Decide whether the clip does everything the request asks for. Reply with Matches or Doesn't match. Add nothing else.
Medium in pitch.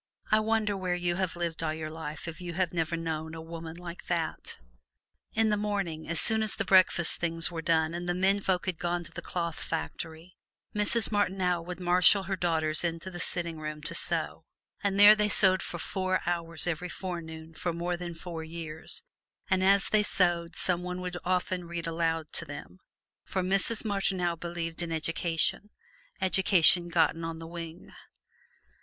Matches